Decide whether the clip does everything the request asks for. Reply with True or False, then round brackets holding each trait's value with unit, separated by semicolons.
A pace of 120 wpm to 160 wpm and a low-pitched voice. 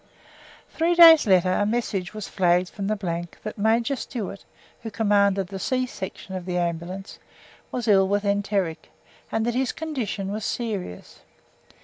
False (150 wpm; 200 Hz)